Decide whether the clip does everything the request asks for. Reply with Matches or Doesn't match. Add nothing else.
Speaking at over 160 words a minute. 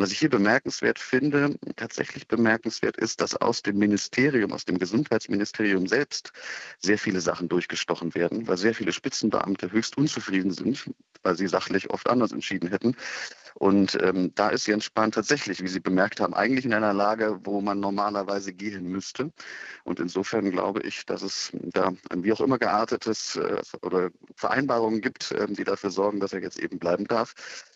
Matches